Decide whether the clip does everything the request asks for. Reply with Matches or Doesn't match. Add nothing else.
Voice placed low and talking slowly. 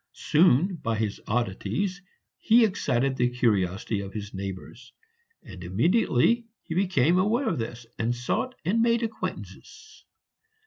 Matches